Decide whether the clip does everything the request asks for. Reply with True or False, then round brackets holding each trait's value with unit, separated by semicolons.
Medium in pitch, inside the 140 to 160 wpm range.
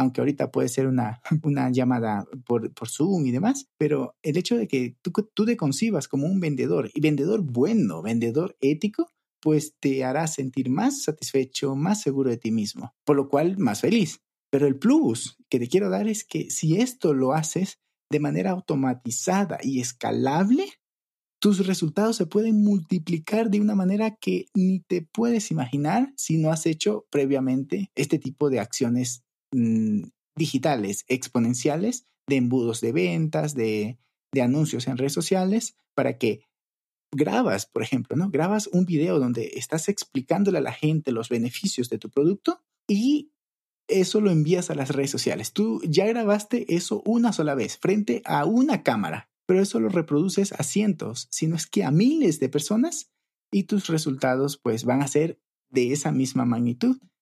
False (160 Hz; 170 wpm)